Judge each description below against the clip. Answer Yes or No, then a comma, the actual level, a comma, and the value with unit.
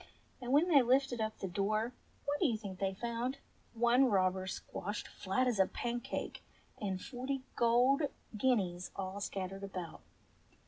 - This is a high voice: Yes, high, 225 Hz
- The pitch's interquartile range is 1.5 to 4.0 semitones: No, average, 4.7 semitones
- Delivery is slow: No, average, 155 wpm